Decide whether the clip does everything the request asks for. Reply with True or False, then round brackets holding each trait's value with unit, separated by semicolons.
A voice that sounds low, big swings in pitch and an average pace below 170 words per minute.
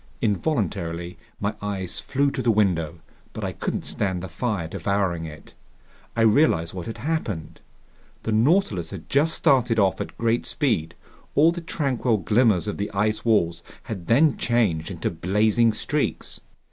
True (105 Hz; 5.7 semitones; 155 wpm)